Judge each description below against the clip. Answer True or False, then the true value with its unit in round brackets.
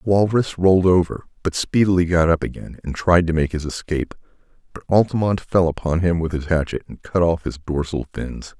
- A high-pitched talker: False (85 Hz)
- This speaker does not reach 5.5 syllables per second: False (5.7 syllables/s)